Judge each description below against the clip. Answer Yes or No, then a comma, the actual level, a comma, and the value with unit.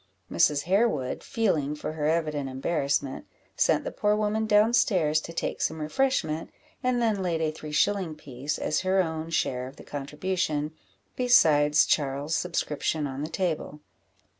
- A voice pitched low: No, medium, 155 Hz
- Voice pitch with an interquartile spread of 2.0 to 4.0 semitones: No, average, 4.6 semitones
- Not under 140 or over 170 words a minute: Yes, average, 155 wpm